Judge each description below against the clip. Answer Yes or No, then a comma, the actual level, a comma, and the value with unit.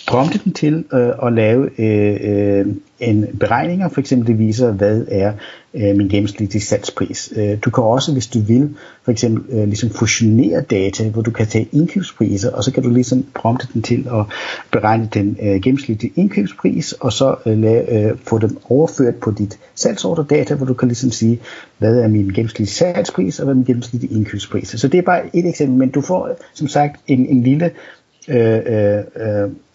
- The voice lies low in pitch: Yes, low, 120 Hz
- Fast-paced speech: No, average, 195 wpm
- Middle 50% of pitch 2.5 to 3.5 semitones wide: No, average, 3.9 semitones